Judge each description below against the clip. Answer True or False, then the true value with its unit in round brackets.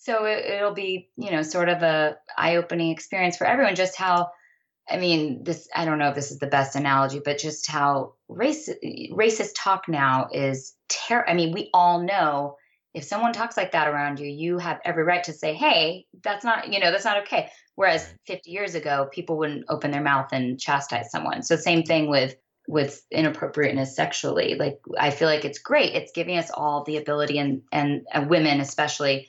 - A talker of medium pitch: True (160 Hz)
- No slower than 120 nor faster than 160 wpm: False (200 wpm)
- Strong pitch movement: False (4.3 semitones)